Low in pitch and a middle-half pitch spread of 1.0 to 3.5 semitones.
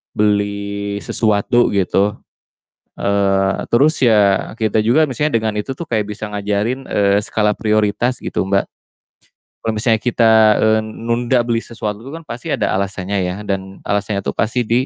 Yes: low, 105 Hz; narrow, 2.5 semitones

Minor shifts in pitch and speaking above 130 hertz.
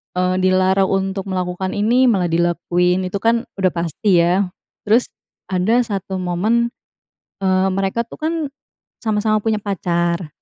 No: average, 3.0 semitones; high, 190 Hz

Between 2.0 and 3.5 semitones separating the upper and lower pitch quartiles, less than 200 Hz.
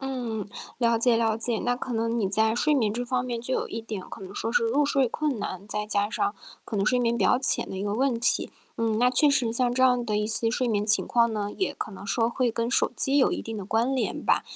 No: narrow, 2.5 semitones; high, 230 Hz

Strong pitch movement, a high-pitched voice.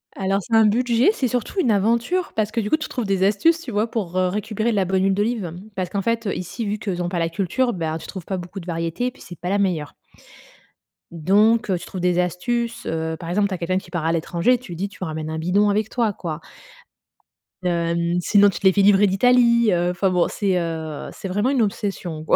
No: average, 4.1 semitones; high, 195 Hz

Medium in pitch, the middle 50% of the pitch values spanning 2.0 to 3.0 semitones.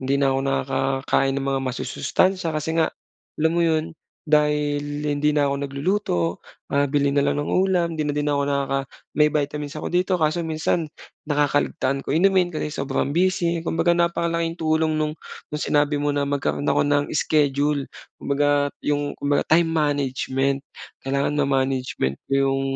Yes: medium, 145 Hz; narrow, 2.4 semitones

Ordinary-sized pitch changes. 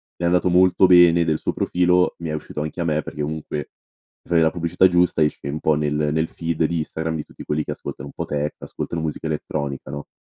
No: narrow, 2.3 semitones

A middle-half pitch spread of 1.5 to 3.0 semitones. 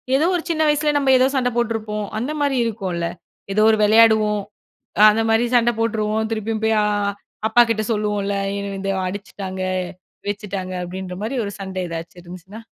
Yes: narrow, 2.6 semitones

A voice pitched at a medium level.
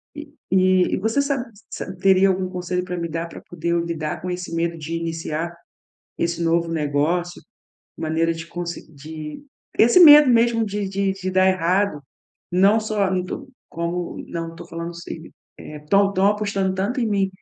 Yes: medium, 180 Hz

